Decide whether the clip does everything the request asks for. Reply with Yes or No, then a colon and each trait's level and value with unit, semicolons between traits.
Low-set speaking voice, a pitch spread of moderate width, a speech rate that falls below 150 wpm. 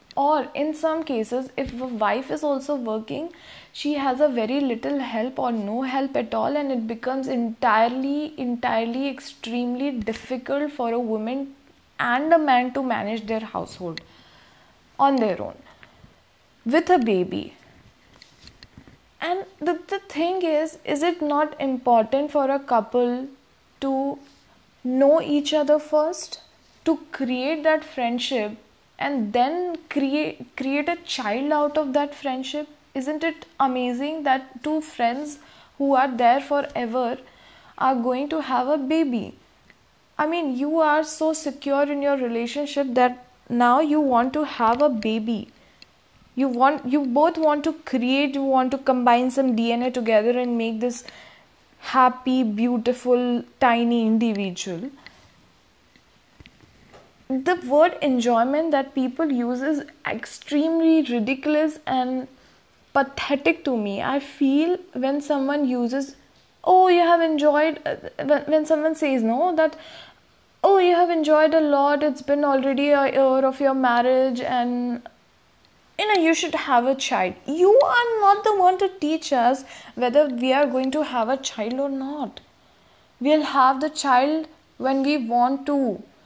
No: very high, 275 Hz; average, 3.4 semitones; average, 140 wpm